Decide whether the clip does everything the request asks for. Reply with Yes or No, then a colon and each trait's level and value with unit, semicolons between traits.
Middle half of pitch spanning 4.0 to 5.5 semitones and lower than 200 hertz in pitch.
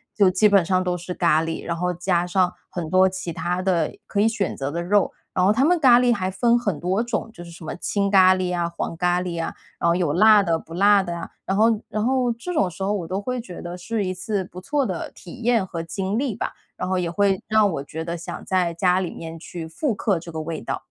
No: average, 3.2 semitones; medium, 185 Hz